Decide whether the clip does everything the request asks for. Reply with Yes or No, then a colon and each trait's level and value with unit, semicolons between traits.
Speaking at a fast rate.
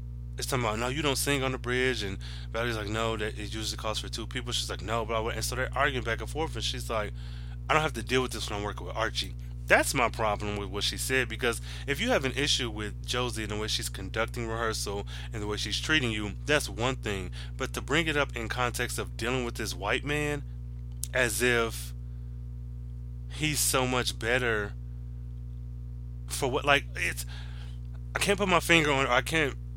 Yes: fast, 220 wpm